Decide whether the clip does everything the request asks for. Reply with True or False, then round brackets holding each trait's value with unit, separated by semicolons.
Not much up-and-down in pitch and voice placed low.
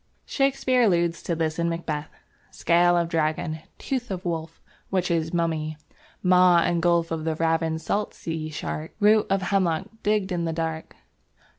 False (2.3 semitones; 170 Hz)